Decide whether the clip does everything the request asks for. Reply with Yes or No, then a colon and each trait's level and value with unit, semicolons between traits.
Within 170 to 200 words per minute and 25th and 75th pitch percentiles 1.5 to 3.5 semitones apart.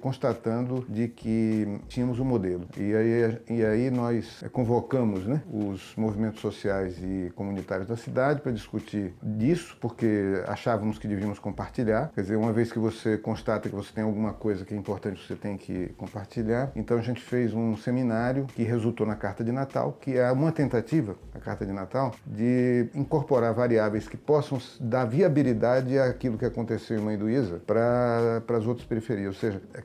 Yes: average, 175 wpm; average, 2.9 semitones